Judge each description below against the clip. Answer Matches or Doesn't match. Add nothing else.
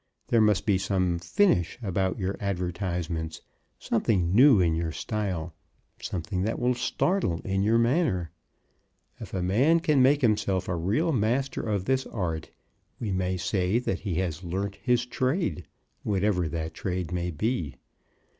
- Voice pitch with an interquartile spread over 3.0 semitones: Matches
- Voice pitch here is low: Matches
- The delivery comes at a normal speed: Matches